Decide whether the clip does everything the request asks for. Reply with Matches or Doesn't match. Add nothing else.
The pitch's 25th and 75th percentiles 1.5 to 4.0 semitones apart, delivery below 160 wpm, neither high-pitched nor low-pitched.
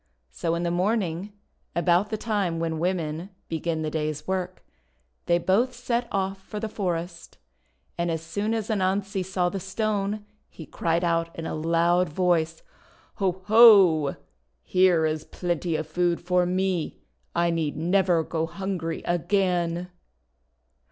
Matches